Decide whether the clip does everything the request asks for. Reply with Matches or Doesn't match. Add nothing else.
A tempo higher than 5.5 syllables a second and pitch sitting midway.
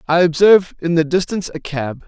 Matches